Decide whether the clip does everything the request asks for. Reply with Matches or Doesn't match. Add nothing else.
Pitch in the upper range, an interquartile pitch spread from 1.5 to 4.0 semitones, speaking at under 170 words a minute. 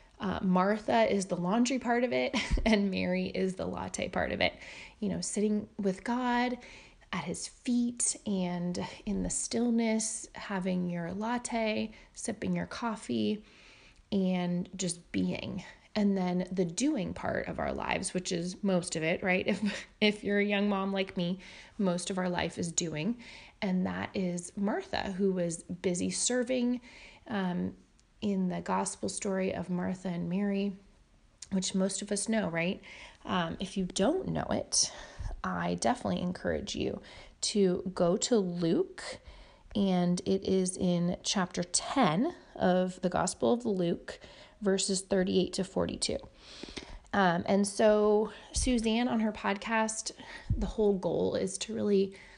Matches